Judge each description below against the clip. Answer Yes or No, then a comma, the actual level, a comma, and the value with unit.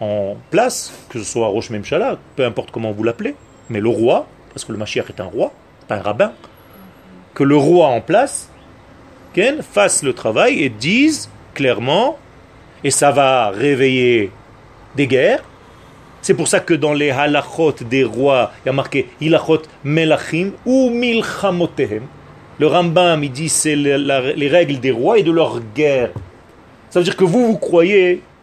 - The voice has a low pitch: No, medium, 145 Hz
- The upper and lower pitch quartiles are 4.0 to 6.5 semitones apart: Yes, average, 4.7 semitones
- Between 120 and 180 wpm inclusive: Yes, average, 165 wpm